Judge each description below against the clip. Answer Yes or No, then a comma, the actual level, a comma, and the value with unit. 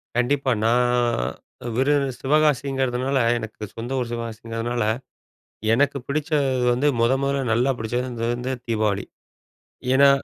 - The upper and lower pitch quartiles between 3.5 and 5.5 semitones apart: No, average, 2.9 semitones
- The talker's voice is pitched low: Yes, low, 125 Hz